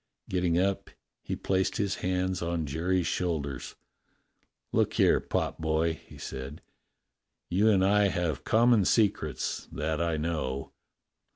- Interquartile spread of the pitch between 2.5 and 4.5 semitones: Yes, average, 3.4 semitones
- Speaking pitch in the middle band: No, very low, 85 Hz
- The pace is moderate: No, slow, 125 wpm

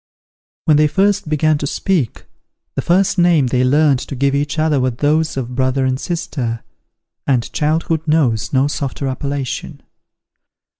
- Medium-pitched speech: Yes, medium, 145 Hz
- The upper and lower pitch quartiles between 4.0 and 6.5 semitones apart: No, average, 3.3 semitones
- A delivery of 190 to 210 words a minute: No, average, 150 wpm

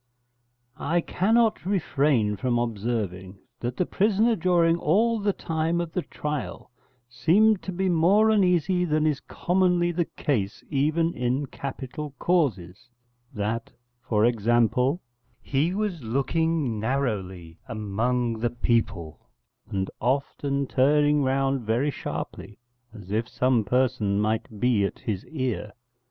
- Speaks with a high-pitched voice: No, low, 135 Hz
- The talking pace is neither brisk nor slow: No, slow, 125 wpm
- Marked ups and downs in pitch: Yes, wide, 7.0 semitones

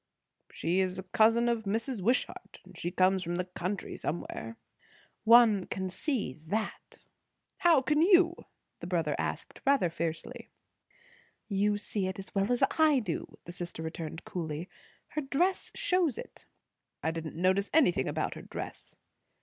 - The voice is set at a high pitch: Yes, high, 195 Hz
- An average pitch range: No, wide, 6.1 semitones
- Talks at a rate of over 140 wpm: Yes, average, 150 wpm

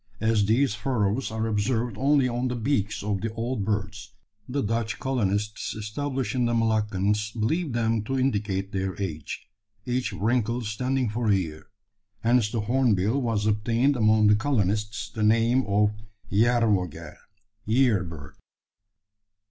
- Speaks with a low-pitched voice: Yes, low, 110 Hz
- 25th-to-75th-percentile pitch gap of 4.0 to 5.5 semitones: No, average, 3.0 semitones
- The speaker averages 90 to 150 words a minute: Yes, average, 140 wpm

